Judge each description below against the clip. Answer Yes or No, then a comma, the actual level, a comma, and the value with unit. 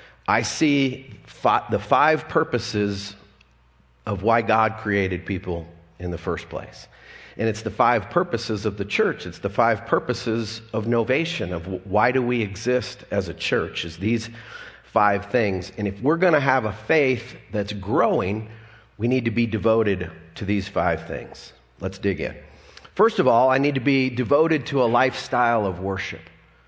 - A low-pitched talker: Yes, low, 110 Hz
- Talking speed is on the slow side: No, average, 170 wpm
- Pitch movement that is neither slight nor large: Yes, average, 3.9 semitones